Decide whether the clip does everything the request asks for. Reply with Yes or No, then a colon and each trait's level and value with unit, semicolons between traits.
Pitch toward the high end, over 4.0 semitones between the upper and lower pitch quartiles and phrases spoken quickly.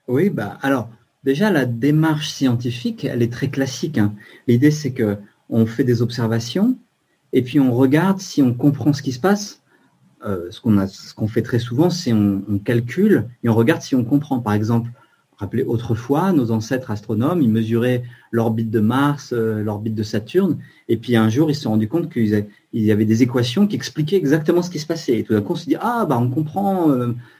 No: low, 125 Hz; average, 4.6 semitones; fast, 220 wpm